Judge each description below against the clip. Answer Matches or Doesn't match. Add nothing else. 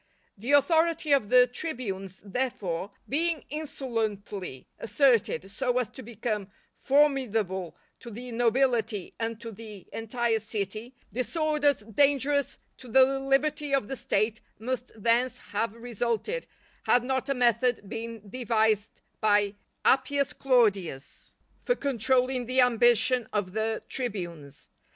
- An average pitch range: Matches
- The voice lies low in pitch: Doesn't match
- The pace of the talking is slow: Matches